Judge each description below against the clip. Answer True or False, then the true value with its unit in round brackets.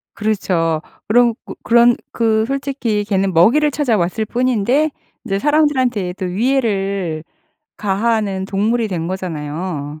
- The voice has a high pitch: True (210 Hz)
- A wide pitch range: False (4.5 semitones)